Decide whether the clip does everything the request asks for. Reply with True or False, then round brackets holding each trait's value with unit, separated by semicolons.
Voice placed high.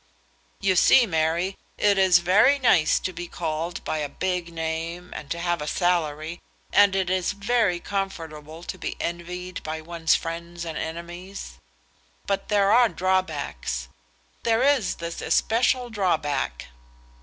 False (175 Hz)